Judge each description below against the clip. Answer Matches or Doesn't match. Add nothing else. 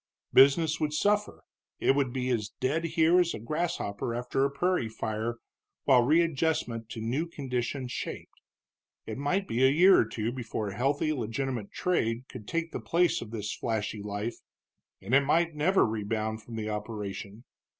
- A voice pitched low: Matches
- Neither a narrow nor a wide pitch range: Doesn't match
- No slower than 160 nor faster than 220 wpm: Matches